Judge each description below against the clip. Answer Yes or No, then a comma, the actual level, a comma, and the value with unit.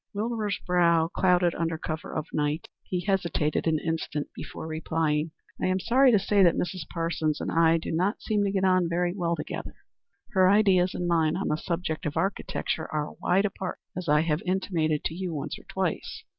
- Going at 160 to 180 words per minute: No, average, 200 wpm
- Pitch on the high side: No, medium, 170 Hz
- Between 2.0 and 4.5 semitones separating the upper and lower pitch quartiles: Yes, average, 3.0 semitones